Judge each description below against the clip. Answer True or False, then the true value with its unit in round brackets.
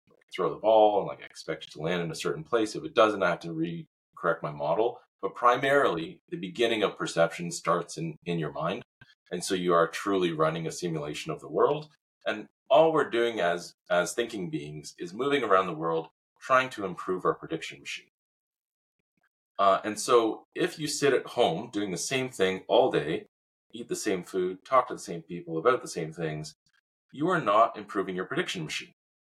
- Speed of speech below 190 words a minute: False (200 wpm)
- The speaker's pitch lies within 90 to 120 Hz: True (95 Hz)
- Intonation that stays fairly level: False (6.3 semitones)